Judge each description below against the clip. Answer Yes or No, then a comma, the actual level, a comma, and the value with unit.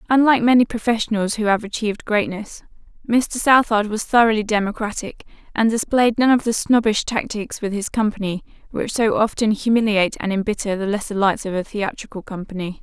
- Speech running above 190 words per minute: No, average, 165 wpm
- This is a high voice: Yes, high, 215 Hz